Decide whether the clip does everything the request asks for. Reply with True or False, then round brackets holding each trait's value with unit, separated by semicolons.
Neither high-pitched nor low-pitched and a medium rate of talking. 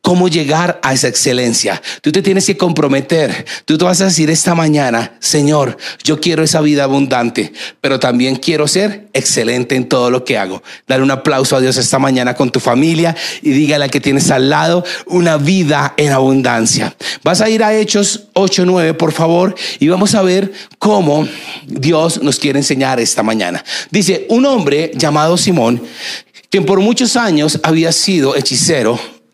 True (155 Hz; 175 wpm)